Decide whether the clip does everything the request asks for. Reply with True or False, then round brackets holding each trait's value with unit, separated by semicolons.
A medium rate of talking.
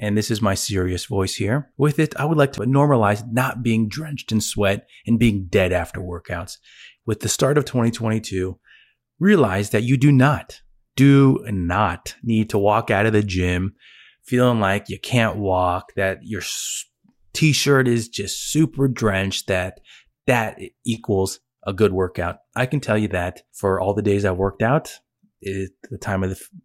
True (180 wpm)